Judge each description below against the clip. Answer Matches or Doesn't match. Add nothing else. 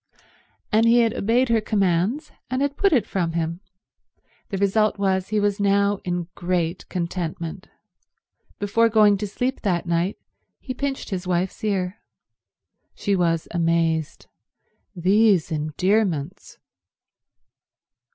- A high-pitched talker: Matches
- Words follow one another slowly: Matches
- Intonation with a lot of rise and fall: Doesn't match